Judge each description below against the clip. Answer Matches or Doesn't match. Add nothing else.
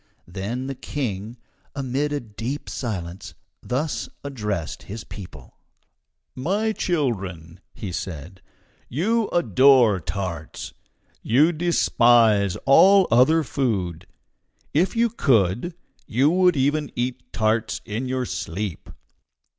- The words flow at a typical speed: Doesn't match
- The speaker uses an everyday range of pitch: Doesn't match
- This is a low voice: Matches